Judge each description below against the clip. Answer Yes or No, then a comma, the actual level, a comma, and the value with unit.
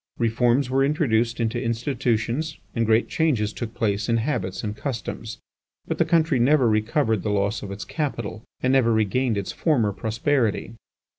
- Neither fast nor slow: Yes, average, 160 wpm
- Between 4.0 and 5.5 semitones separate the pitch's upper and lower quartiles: No, average, 3.5 semitones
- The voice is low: Yes, low, 115 Hz